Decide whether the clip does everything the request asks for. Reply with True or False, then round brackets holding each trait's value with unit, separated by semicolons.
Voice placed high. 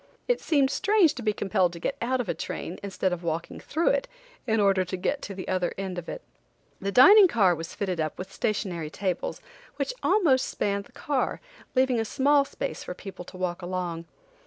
True (200 Hz)